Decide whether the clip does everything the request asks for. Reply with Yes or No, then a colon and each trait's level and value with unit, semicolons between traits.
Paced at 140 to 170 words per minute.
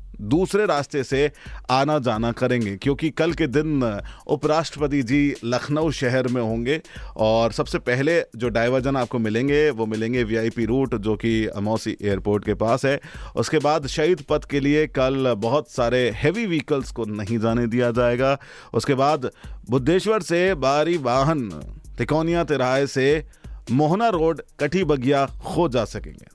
Yes: average, 150 wpm